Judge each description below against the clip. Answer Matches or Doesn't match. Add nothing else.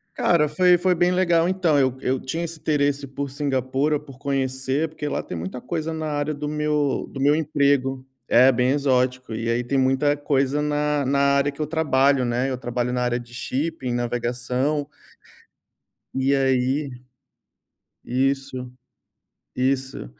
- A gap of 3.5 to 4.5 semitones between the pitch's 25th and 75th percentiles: Doesn't match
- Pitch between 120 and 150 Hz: Matches